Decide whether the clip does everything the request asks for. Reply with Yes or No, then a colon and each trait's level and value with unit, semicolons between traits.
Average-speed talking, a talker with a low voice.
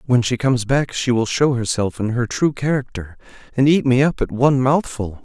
No: fast, 220 wpm; low, 125 Hz